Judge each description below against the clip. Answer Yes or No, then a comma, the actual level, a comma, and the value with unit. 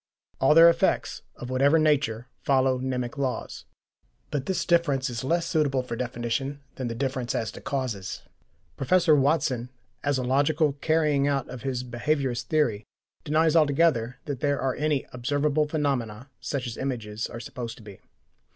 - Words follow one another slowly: No, average, 160 wpm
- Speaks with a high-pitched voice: No, low, 135 Hz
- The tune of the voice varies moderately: Yes, average, 3.4 semitones